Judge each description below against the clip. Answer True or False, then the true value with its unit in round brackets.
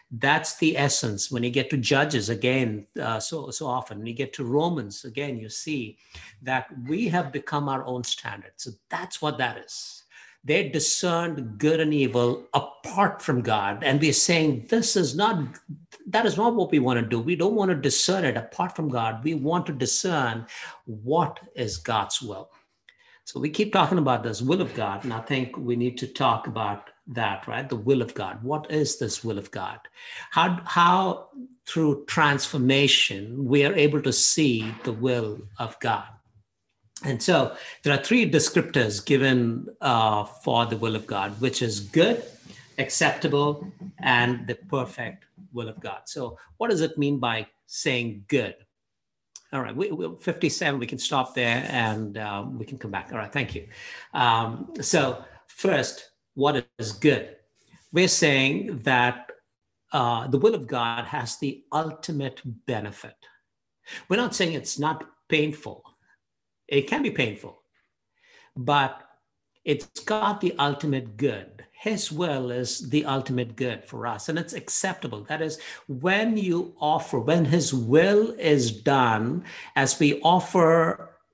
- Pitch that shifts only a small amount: False (4.9 semitones)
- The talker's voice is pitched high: False (135 Hz)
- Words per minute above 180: False (165 wpm)